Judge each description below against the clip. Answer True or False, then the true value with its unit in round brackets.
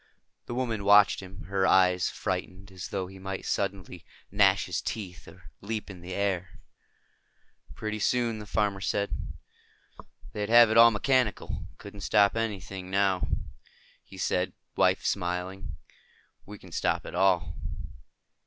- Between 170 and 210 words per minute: False (145 wpm)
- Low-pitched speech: True (95 Hz)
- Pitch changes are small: True (2.1 semitones)